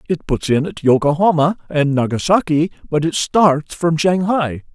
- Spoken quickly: No, average, 150 wpm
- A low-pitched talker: No, medium, 160 Hz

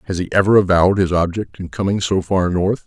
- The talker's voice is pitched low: Yes, very low, 95 Hz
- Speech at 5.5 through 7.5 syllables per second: Yes, 6.0 syllables/s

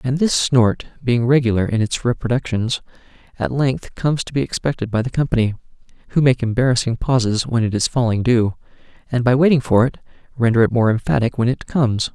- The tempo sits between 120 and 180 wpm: No, average, 190 wpm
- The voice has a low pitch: Yes, low, 120 Hz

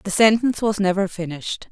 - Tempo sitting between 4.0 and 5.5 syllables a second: No, 6.0 syllables/s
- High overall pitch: Yes, high, 200 Hz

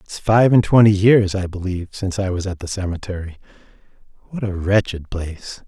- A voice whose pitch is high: No, very low, 95 Hz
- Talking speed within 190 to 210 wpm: No, average, 180 wpm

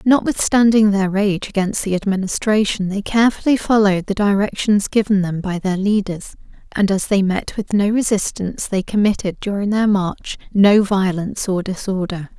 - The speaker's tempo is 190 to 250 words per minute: No, average, 155 wpm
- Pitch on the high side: Yes, high, 200 Hz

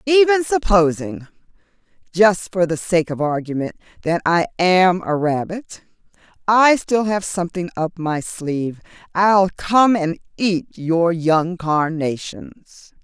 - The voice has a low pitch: No, medium, 180 Hz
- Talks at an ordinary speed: No, slow, 115 wpm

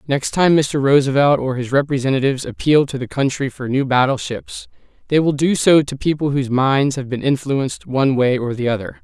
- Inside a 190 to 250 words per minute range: Yes, average, 200 wpm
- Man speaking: Yes, male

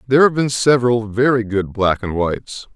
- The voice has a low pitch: Yes, low, 115 Hz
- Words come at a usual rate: Yes, average, 195 wpm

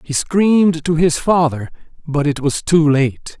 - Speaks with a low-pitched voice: No, medium, 155 Hz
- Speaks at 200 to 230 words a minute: No, average, 175 wpm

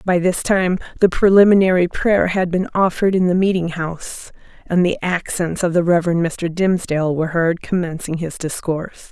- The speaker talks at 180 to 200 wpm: No, average, 170 wpm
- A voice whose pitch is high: No, medium, 175 Hz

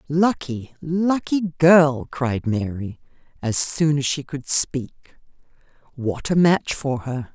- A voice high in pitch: No, medium, 145 Hz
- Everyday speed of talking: No, slow, 130 wpm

